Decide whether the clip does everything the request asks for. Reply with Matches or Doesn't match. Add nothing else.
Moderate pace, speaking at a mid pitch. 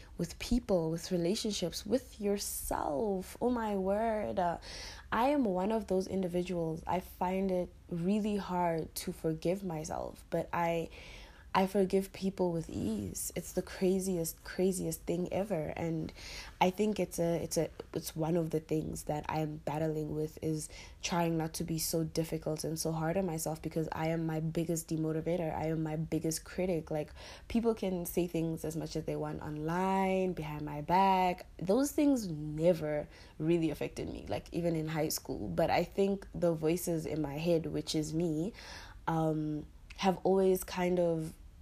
Matches